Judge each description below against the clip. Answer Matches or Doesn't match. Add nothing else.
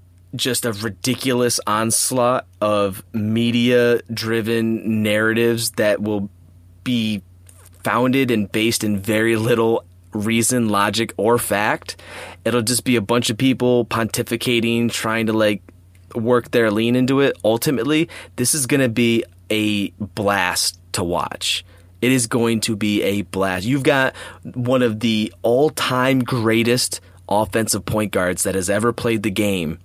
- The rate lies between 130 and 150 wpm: Matches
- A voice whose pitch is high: Doesn't match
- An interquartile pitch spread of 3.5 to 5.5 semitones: Doesn't match